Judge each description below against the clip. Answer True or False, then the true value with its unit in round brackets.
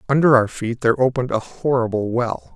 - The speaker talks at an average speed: True (190 wpm)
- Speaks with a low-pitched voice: True (120 Hz)